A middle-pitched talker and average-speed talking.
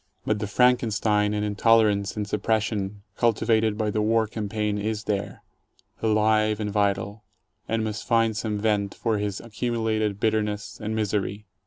No: low, 105 Hz; average, 155 wpm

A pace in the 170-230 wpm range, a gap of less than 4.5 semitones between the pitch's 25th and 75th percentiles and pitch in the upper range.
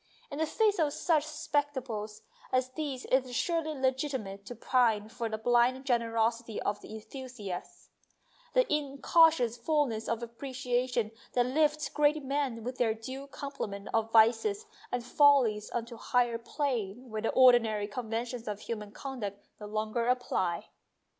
No: average, 155 wpm; average, 3.9 semitones; high, 245 Hz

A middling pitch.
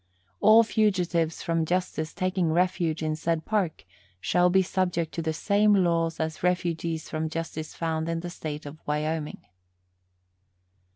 Yes: medium, 165 Hz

